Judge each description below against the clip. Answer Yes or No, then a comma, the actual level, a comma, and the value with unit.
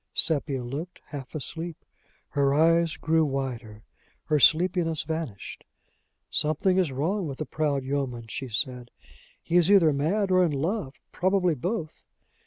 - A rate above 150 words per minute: No, average, 140 wpm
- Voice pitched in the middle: Yes, medium, 155 Hz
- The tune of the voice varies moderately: Yes, average, 4.1 semitones